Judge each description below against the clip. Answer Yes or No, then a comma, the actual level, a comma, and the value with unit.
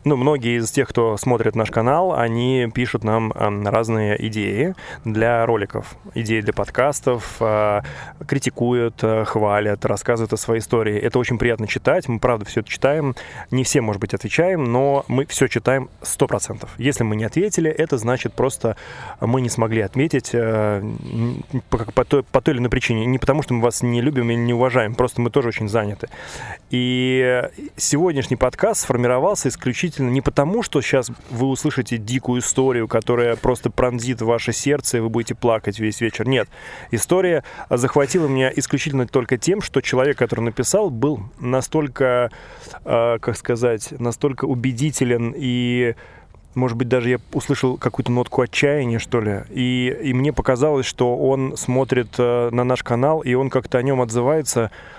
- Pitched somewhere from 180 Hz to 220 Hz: No, low, 125 Hz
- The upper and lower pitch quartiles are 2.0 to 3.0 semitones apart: Yes, narrow, 2.5 semitones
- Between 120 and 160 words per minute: Yes, average, 155 wpm